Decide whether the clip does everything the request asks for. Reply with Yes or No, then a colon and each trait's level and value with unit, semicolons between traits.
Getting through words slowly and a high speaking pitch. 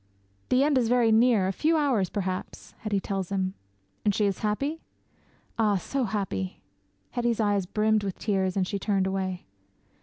No: average, 170 wpm; high, 205 Hz